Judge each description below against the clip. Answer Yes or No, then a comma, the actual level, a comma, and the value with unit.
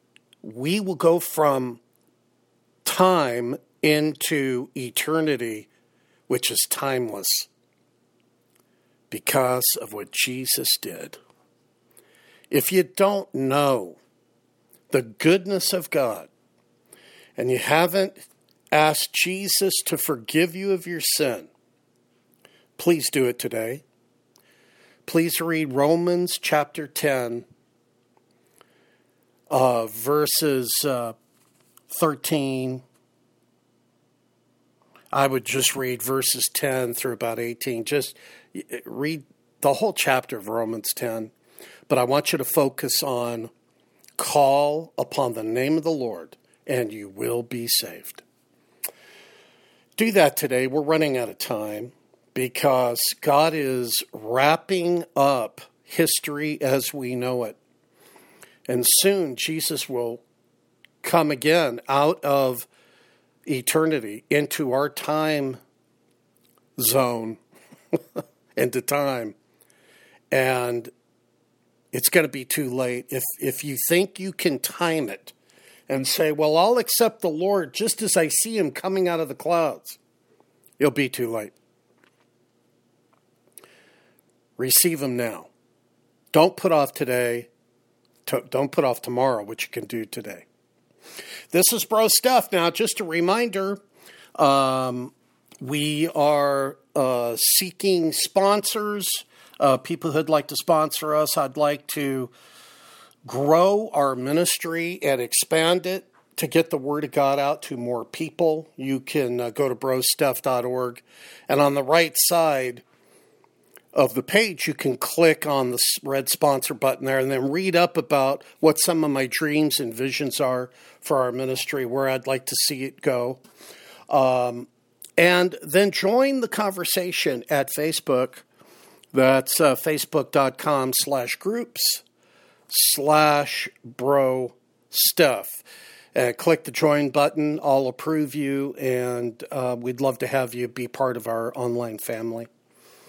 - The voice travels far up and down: No, average, 4.5 semitones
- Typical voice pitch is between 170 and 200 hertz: No, medium, 140 Hz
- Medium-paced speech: No, slow, 120 wpm